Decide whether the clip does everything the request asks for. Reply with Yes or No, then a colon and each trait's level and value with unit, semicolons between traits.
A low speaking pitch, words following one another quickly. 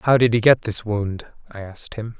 Yes: low, 110 Hz; fast, 245 wpm